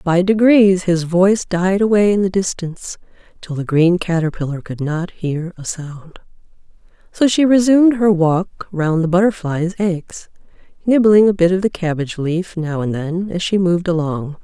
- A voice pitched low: No, medium, 180 Hz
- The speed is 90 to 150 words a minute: No, average, 170 wpm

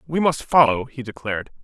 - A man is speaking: Yes, male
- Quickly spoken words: No, average, 185 wpm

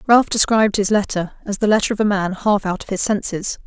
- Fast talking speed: Yes, fast, 245 wpm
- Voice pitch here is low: No, high, 205 Hz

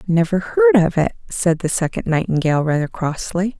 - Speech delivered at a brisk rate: No, average, 165 wpm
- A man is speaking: No, female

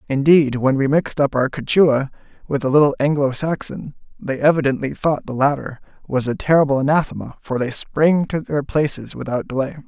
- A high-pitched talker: No, medium, 140 Hz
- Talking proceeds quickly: No, average, 175 wpm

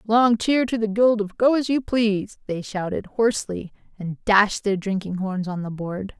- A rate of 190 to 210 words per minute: Yes, fast, 205 wpm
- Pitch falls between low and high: No, high, 210 Hz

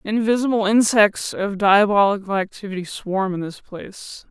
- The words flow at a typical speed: No, slow, 125 wpm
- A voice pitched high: Yes, high, 200 Hz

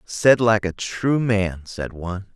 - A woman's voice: No, male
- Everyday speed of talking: Yes, average, 180 wpm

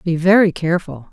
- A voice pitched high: No, medium, 175 Hz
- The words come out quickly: No, average, 160 wpm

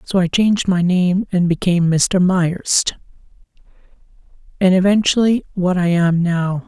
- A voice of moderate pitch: Yes, medium, 180 Hz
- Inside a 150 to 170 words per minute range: No, slow, 135 wpm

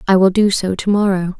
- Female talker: Yes, female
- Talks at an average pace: No, fast, 260 wpm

